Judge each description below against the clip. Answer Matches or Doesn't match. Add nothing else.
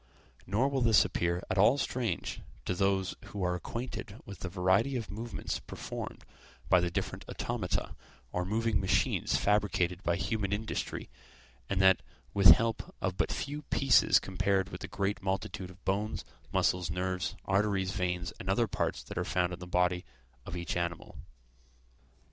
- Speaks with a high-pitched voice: Doesn't match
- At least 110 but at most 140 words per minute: Doesn't match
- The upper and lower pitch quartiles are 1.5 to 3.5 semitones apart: Matches